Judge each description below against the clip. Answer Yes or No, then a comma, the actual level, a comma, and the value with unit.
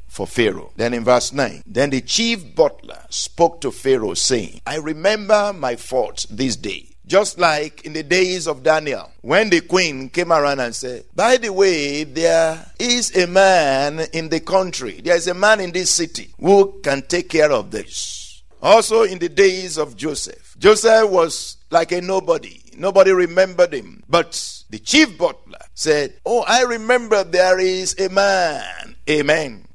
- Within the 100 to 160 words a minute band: No, average, 170 wpm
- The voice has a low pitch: No, medium, 180 Hz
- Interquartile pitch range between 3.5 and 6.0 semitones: Yes, average, 4.6 semitones